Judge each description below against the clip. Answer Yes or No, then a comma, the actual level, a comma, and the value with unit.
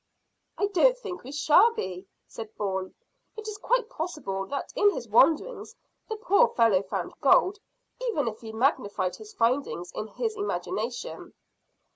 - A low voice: No, very high, 295 Hz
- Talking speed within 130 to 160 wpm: Yes, average, 150 wpm